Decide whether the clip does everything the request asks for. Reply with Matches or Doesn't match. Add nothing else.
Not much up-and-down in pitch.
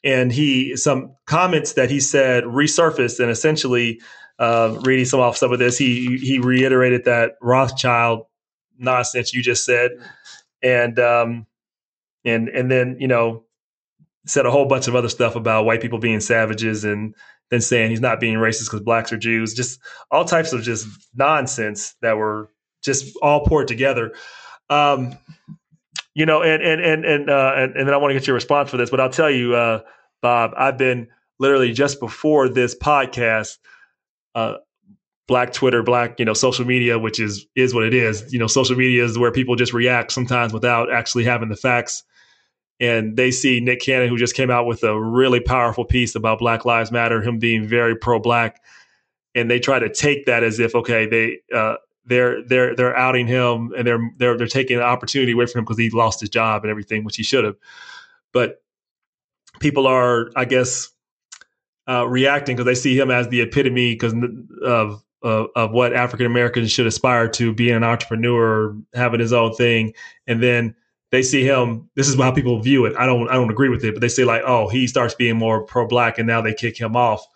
Matches